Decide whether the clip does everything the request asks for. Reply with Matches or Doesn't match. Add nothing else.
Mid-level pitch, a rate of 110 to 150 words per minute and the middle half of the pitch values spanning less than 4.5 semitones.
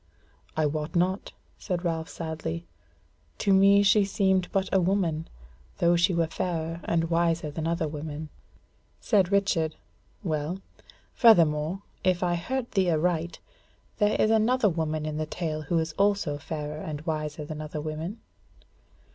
Matches